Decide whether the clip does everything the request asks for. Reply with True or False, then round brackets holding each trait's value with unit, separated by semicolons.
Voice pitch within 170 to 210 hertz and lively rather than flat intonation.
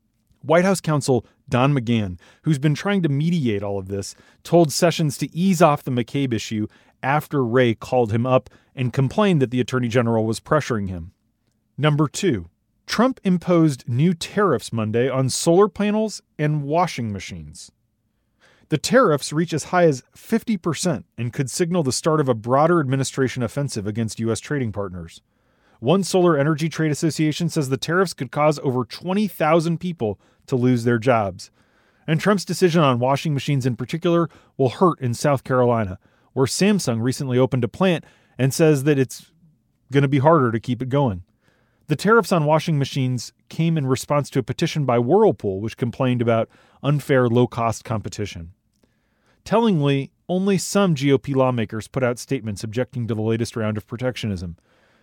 False (130 Hz; 5.7 semitones)